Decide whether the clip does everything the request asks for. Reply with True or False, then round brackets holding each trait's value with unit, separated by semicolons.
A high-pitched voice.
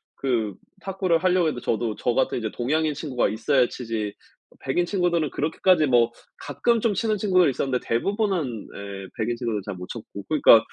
False (135 Hz)